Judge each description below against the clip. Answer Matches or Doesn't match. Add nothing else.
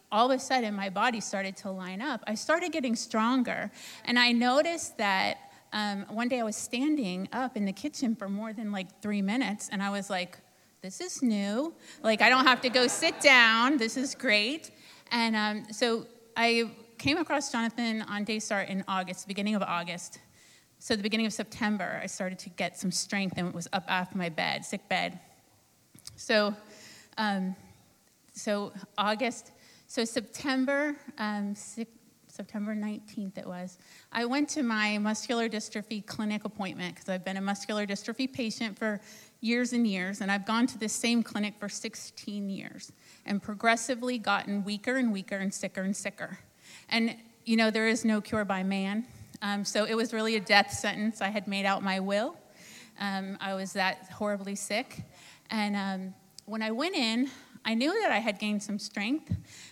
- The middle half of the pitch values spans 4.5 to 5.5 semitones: Doesn't match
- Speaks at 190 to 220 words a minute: Doesn't match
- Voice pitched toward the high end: Matches